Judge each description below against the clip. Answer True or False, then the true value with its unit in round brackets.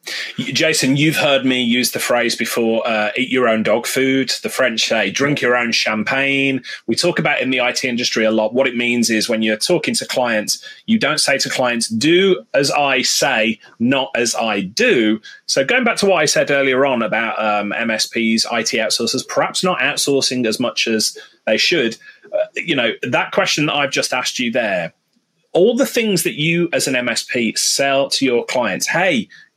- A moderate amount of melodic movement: False (7.5 semitones)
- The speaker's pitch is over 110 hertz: True (135 Hz)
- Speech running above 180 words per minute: True (200 wpm)